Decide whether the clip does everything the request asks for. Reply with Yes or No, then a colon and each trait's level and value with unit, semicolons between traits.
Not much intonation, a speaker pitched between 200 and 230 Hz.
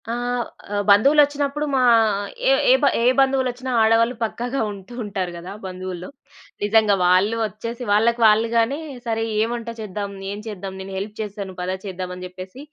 No: average, 4.0 semitones; high, 215 Hz